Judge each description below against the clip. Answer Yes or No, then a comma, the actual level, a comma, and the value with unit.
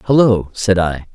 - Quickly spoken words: No, average, 155 wpm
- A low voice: Yes, low, 100 Hz